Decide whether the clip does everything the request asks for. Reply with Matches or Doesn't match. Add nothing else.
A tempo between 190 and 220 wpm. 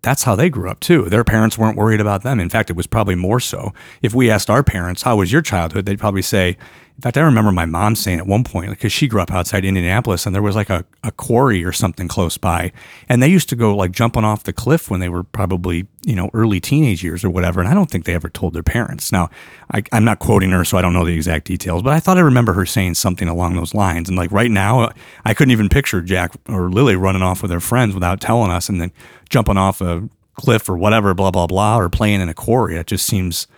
Doesn't match